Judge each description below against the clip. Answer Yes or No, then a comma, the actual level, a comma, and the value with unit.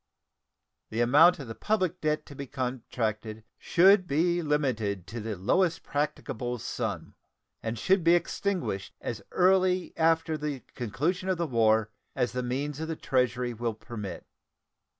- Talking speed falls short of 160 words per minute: Yes, average, 150 wpm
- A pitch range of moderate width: No, wide, 6.5 semitones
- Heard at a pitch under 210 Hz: Yes, medium, 140 Hz